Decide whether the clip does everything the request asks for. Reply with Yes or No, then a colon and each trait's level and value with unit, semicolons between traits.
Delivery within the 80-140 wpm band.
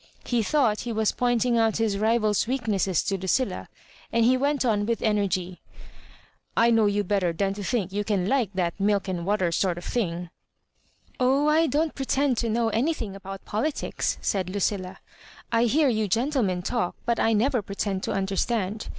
No: average, 185 wpm